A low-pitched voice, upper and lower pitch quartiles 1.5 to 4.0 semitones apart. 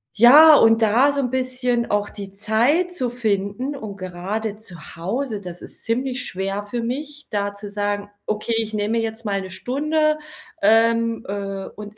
No: high, 220 Hz; average, 3.7 semitones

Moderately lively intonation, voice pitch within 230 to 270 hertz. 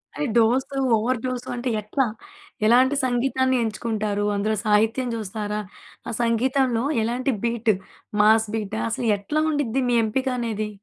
Yes: average, 3.2 semitones; high, 235 Hz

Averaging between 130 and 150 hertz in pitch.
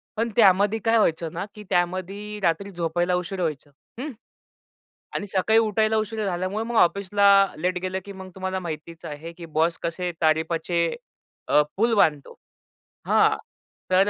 No: medium, 185 Hz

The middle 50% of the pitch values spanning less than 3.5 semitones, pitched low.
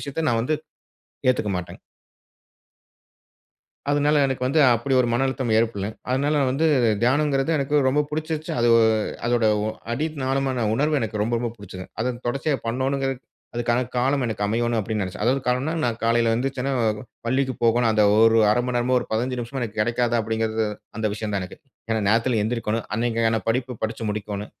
Yes: average, 3.1 semitones; low, 120 Hz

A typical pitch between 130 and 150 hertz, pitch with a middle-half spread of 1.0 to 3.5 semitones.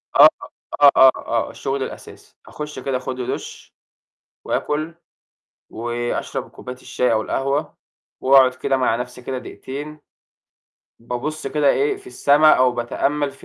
Yes: low, 135 Hz; average, 2.8 semitones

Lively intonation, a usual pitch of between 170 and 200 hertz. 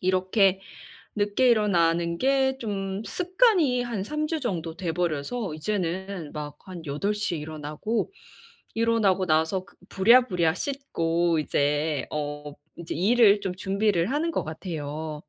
Yes: wide, 5.8 semitones; medium, 185 Hz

